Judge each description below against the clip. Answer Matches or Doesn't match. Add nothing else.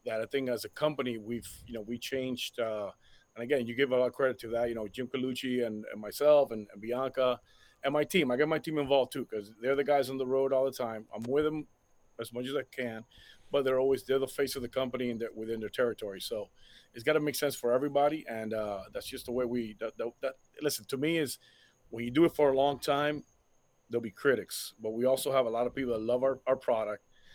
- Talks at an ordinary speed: Doesn't match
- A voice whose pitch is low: Matches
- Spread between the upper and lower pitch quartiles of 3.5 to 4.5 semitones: Doesn't match